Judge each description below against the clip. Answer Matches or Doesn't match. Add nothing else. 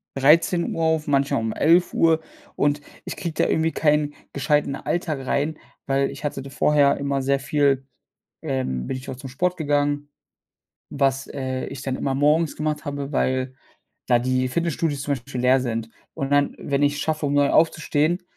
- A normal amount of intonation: Doesn't match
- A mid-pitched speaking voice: Matches